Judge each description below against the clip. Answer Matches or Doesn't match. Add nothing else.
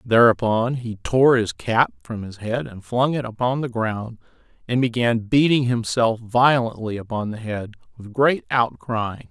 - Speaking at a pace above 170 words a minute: Doesn't match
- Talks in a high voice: Doesn't match